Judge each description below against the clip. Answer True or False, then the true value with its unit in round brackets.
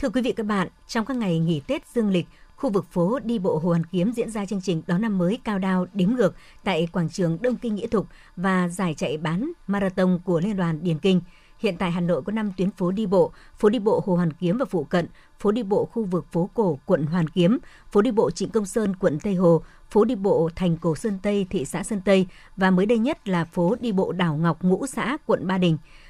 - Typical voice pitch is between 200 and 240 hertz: False (190 Hz)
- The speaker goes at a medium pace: False (260 wpm)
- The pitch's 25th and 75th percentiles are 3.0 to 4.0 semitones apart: True (3.7 semitones)